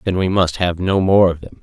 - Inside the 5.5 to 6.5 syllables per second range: No, 5.3 syllables/s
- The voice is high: No, very low, 90 Hz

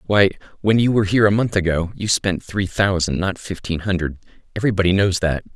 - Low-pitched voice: Yes, very low, 95 Hz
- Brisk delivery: No, average, 195 wpm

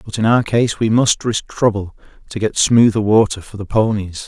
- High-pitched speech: No, low, 110 Hz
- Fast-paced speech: Yes, fast, 210 wpm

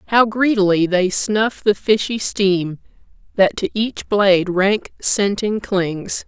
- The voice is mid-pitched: No, high, 200 Hz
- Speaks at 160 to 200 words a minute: No, slow, 135 wpm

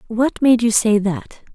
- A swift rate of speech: No, average, 195 wpm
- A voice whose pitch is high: Yes, high, 220 Hz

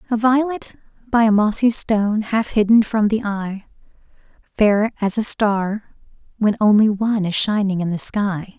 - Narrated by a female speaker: Yes, female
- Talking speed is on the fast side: No, average, 160 wpm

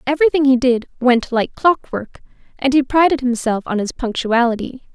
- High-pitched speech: Yes, very high, 255 Hz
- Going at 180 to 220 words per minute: No, average, 160 wpm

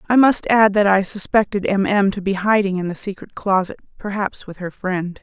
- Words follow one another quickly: Yes, fast, 220 wpm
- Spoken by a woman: Yes, female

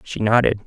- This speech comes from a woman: No, male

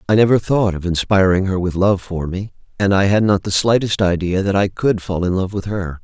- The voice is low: Yes, very low, 95 Hz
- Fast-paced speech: Yes, fast, 250 wpm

